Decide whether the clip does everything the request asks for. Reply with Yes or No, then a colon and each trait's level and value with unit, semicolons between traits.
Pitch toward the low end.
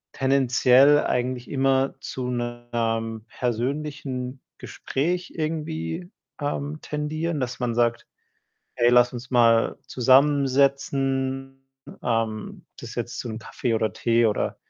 Yes: low, 125 Hz